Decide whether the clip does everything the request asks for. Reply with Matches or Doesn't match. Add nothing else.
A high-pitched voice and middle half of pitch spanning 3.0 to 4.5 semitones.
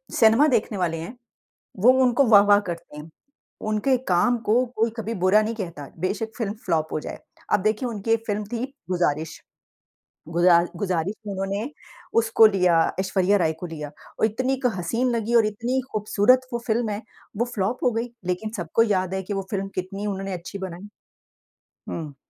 Matches